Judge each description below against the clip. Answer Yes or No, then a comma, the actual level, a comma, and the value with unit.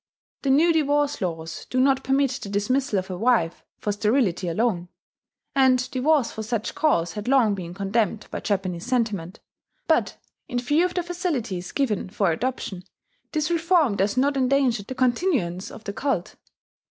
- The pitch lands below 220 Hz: No, high, 240 Hz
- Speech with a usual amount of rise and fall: No, wide, 5.8 semitones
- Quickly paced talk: No, average, 165 wpm